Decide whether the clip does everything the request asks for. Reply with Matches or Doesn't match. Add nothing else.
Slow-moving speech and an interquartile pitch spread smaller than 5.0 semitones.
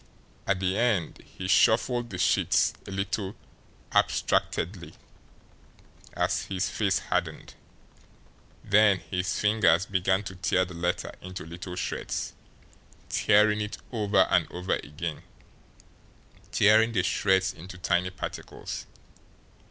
Matches